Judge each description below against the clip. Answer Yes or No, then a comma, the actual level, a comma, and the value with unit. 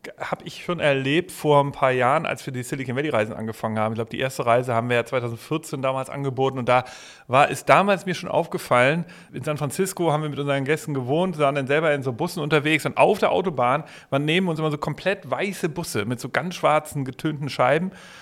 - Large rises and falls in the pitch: No, average, 3.5 semitones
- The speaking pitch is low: No, medium, 145 Hz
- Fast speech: Yes, fast, 225 wpm